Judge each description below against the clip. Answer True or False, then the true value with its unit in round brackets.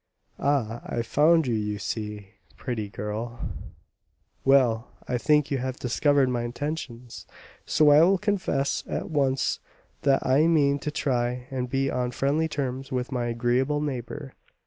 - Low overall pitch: True (130 Hz)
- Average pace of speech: True (155 wpm)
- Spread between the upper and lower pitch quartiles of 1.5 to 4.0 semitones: True (3.4 semitones)